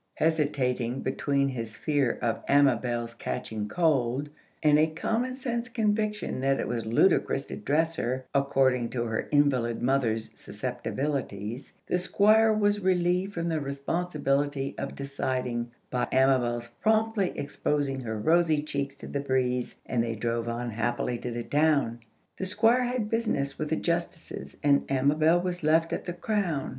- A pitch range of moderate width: No, wide, 5.8 semitones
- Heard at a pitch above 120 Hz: Yes, medium, 140 Hz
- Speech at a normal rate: Yes, average, 150 wpm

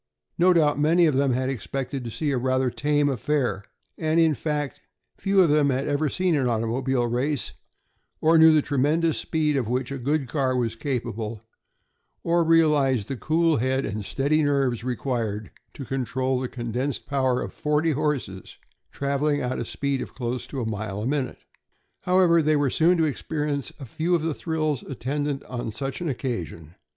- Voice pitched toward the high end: No, medium, 140 Hz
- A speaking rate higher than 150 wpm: Yes, average, 180 wpm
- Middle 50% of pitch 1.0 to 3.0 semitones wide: No, average, 3.5 semitones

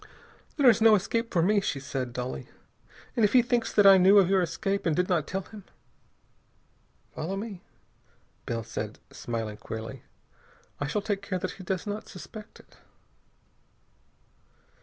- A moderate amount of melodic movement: No, wide, 6.0 semitones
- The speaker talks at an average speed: Yes, average, 160 wpm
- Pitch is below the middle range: No, high, 190 Hz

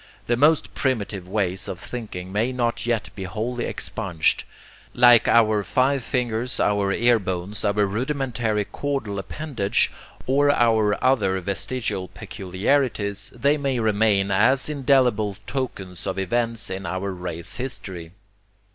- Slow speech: Yes, slow, 130 wpm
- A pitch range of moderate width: Yes, average, 4.4 semitones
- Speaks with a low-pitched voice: Yes, low, 110 Hz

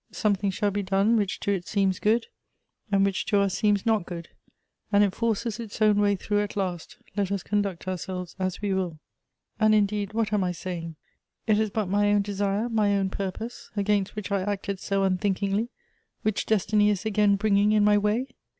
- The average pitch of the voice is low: No, high, 200 Hz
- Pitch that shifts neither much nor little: No, narrow, 1.5 semitones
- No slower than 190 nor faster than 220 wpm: Yes, average, 200 wpm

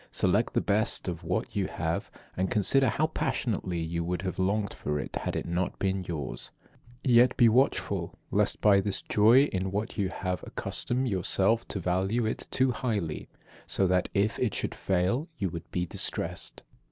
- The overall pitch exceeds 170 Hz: No, very low, 95 Hz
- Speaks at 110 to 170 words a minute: No, average, 180 wpm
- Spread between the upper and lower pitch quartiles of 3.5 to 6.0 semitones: Yes, average, 3.9 semitones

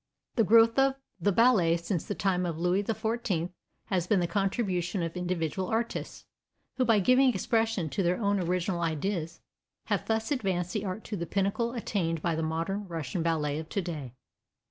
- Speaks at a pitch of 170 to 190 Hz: Yes, medium, 185 Hz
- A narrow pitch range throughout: No, average, 4.5 semitones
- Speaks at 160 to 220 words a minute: Yes, average, 175 wpm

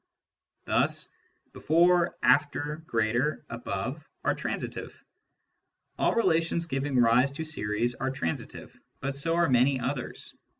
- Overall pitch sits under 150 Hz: Yes, medium, 140 Hz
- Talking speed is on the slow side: Yes, slow, 120 wpm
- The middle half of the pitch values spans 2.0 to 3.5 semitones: No, average, 4.8 semitones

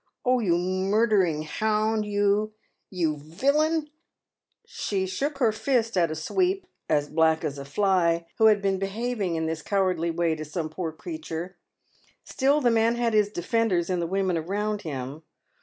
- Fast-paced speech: No, average, 175 wpm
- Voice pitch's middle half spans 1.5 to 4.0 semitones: No, average, 5.1 semitones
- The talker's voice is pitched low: No, high, 195 Hz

